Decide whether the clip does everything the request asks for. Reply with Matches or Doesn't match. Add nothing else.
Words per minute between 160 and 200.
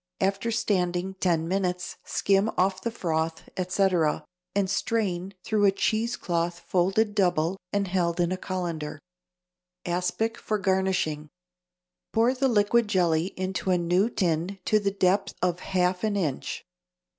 Doesn't match